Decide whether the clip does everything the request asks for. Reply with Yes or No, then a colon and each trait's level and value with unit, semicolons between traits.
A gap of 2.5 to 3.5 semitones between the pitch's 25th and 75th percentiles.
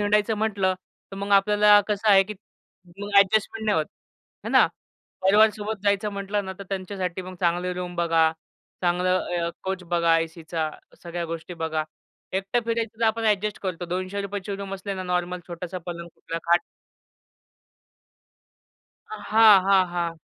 Yes: average, 2.9 semitones